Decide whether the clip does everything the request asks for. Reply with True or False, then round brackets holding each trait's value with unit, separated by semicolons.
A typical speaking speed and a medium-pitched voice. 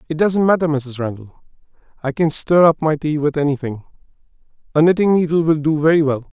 True (180 wpm; 155 Hz)